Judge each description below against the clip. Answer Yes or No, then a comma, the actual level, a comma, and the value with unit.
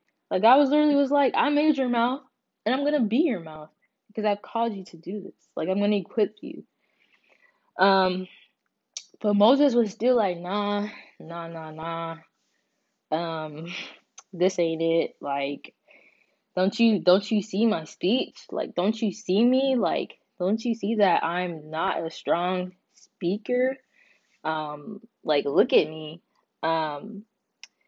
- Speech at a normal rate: Yes, average, 155 wpm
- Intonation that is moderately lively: No, wide, 6.2 semitones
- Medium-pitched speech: No, high, 205 Hz